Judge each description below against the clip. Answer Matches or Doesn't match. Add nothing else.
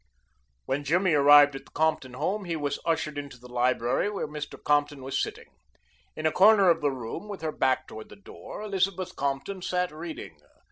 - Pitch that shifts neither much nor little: Matches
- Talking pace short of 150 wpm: Doesn't match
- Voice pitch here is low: Doesn't match